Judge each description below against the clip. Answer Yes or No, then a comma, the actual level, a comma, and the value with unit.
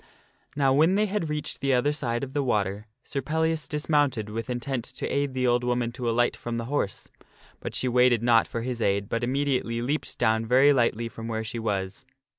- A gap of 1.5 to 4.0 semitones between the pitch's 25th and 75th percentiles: Yes, average, 3.5 semitones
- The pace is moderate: No, fast, 215 wpm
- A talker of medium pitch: No, low, 125 Hz